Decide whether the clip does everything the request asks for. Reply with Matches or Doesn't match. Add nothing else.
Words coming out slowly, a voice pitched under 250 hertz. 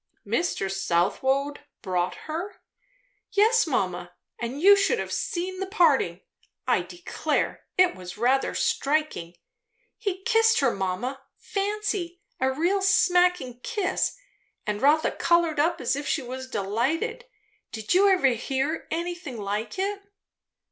Doesn't match